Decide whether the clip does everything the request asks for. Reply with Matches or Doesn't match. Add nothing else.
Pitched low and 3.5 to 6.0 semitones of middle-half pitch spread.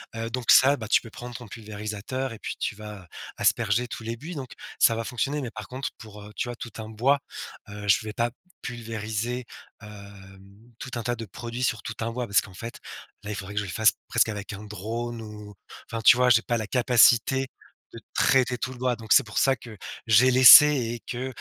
Doesn't match